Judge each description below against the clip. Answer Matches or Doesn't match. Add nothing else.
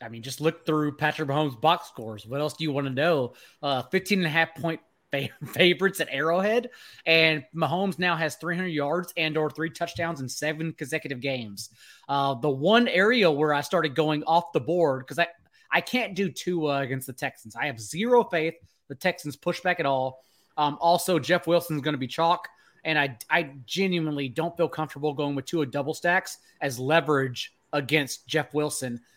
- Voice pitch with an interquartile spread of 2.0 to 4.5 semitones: Matches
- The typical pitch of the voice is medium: Matches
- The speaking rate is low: Doesn't match